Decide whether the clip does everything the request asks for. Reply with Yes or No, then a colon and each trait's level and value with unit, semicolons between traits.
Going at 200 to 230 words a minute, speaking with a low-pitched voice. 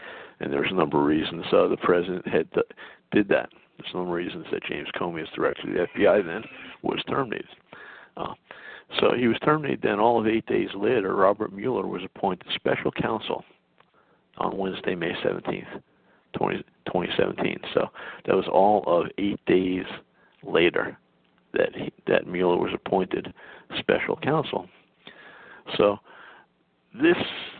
No: average, 150 wpm; low, 115 Hz